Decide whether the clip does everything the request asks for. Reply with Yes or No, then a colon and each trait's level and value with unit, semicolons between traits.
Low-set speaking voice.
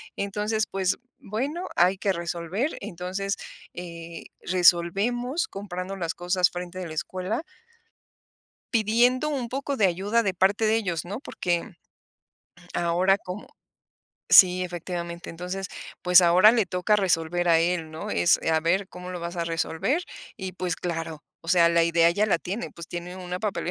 No: medium, 180 Hz